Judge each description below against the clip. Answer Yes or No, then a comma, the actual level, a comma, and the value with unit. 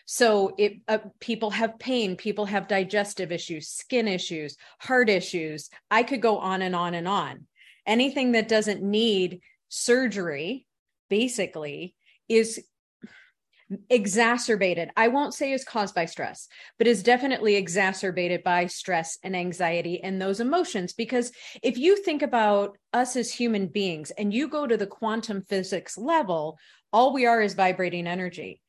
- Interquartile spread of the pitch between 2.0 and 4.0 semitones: No, average, 4.4 semitones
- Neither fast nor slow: Yes, average, 150 wpm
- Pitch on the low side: No, high, 210 Hz